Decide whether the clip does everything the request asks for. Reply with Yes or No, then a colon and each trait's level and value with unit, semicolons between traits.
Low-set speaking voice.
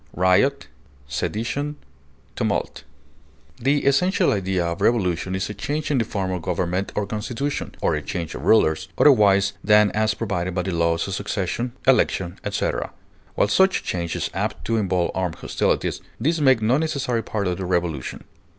Yes: low, 100 Hz